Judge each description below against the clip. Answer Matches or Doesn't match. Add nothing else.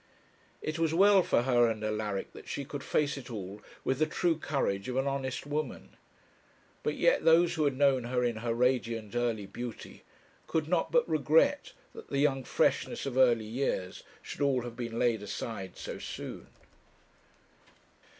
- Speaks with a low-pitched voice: Matches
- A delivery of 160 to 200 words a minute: Matches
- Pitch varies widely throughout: Doesn't match